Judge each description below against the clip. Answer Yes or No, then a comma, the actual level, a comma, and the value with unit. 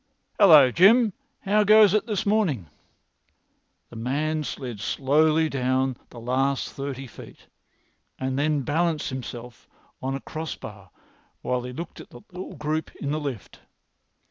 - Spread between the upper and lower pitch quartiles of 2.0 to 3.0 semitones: No, average, 4.1 semitones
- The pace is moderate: Yes, average, 145 wpm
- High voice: No, medium, 145 Hz